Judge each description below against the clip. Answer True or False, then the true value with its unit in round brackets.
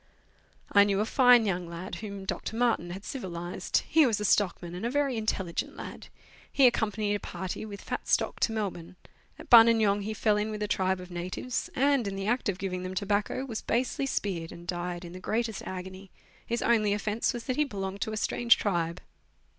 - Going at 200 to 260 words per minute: True (205 wpm)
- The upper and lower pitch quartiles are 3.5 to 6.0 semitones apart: True (3.8 semitones)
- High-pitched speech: True (205 Hz)